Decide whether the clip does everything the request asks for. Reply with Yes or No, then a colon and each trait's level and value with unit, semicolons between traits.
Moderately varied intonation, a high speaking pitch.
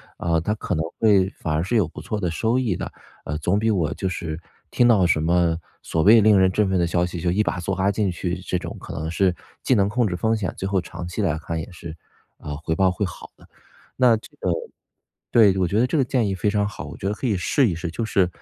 No: average, 3.6 semitones; very low, 95 Hz